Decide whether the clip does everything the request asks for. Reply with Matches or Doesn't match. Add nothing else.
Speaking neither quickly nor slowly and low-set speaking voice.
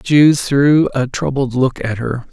Matches